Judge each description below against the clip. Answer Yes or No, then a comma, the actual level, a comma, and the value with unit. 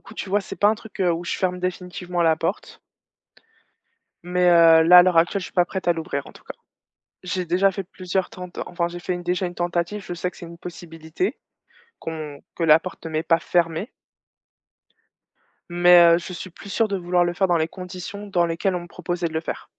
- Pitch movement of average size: No, narrow, 1.5 semitones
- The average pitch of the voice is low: No, medium, 175 Hz